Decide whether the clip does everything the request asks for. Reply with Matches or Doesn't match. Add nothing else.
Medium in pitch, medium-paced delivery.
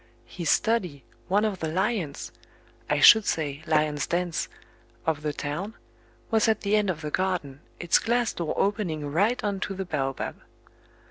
Matches